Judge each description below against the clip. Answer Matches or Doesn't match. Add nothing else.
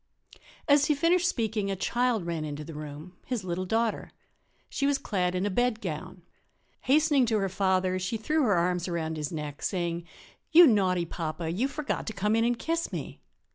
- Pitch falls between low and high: Doesn't match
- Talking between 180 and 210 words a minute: Matches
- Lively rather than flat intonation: Matches